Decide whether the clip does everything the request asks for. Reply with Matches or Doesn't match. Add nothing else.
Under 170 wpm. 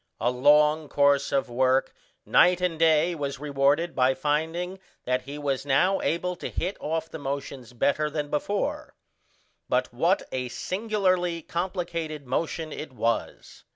Matches